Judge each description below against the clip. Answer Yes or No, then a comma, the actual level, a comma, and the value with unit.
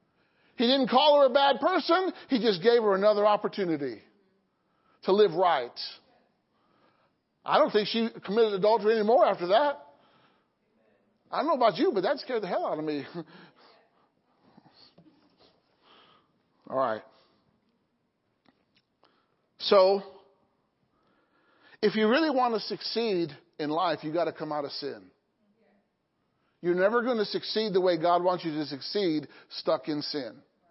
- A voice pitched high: Yes, high, 210 Hz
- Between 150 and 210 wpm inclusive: No, average, 140 wpm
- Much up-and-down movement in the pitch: Yes, wide, 5.9 semitones